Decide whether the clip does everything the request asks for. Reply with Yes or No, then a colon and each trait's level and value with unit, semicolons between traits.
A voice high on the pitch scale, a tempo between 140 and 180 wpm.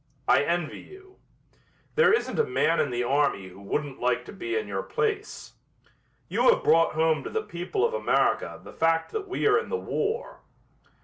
No: high, 200 Hz; average, 190 wpm